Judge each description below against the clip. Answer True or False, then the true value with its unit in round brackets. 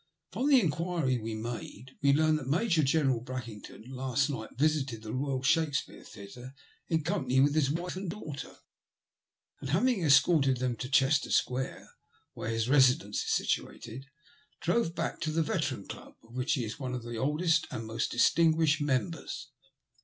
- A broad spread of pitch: False (4.0 semitones)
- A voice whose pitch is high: False (135 Hz)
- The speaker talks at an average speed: True (160 wpm)